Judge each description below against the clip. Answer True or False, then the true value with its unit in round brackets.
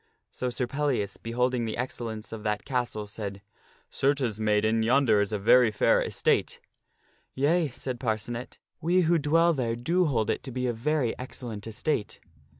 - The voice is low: True (120 Hz)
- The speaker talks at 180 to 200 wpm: True (185 wpm)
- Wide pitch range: False (4.1 semitones)